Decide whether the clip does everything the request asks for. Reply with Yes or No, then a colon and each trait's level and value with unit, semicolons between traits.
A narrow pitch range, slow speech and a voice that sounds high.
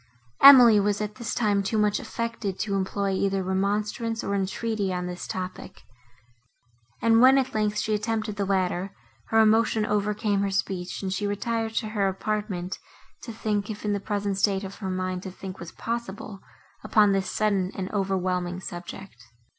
No: narrow, 2.1 semitones; average, 170 wpm; high, 200 Hz